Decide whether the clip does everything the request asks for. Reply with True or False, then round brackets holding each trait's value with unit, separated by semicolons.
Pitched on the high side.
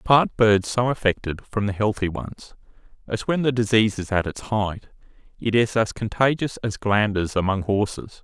False (110 Hz)